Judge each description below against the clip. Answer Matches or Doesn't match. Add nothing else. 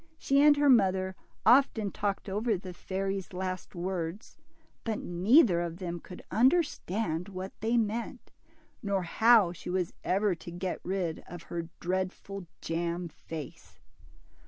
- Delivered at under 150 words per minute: Matches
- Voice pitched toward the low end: Doesn't match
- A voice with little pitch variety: Doesn't match